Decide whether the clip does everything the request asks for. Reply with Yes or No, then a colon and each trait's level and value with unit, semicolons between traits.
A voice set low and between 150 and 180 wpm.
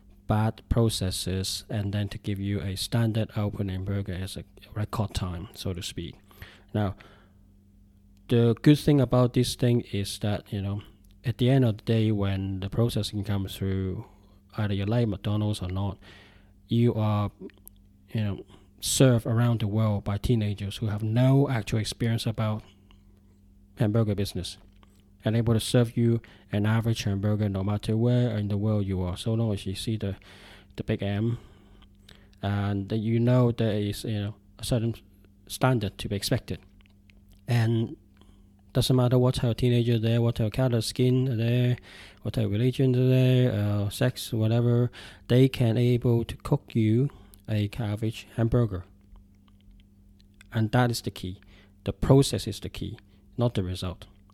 Yes: low, 105 Hz; average, 160 wpm